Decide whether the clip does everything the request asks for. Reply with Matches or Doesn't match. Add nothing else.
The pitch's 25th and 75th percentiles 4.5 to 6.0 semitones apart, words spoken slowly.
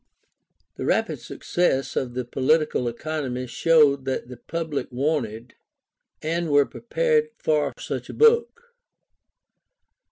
Matches